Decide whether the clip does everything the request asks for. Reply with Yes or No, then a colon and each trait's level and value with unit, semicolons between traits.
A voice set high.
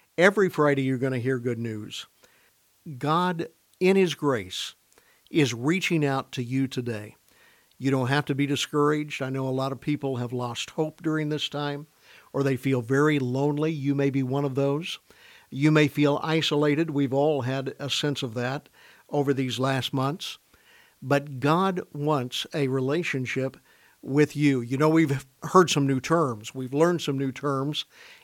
No: medium, 140 Hz